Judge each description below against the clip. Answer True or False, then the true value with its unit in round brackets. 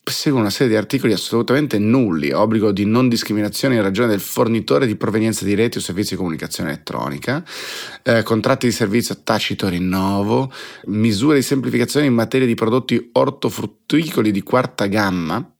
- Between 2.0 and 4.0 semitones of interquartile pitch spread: True (3.4 semitones)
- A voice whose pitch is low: True (110 Hz)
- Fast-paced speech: False (160 wpm)